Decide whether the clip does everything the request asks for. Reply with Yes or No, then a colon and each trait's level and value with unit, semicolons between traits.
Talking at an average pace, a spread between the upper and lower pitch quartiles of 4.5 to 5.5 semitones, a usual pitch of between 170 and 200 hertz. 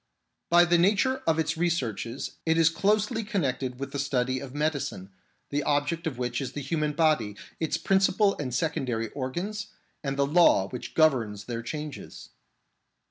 No: average, 165 wpm; average, 4.9 semitones; medium, 145 Hz